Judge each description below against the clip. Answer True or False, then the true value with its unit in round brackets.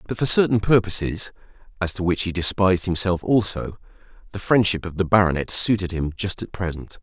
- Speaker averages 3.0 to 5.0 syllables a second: False (5.7 syllables/s)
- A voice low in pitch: True (95 Hz)